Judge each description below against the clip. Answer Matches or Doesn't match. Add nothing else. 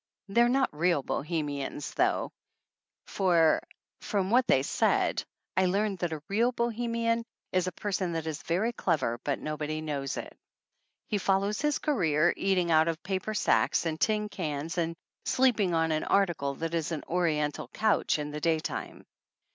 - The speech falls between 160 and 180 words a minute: Matches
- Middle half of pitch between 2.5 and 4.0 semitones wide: Doesn't match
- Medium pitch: Matches